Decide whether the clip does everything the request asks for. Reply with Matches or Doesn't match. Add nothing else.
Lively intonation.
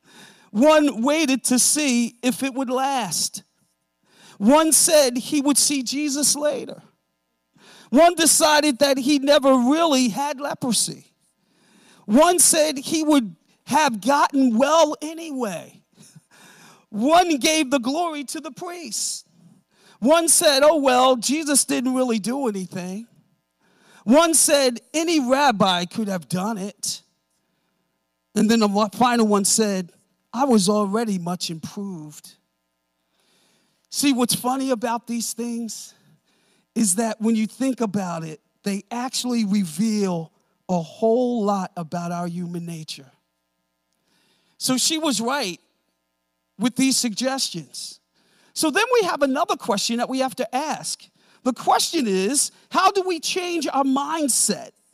Matches